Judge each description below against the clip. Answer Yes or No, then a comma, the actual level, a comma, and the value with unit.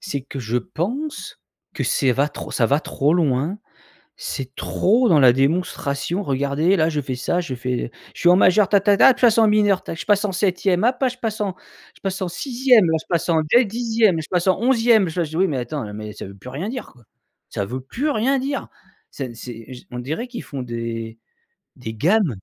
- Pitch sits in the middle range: Yes, medium, 175 Hz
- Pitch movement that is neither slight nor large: No, wide, 8.1 semitones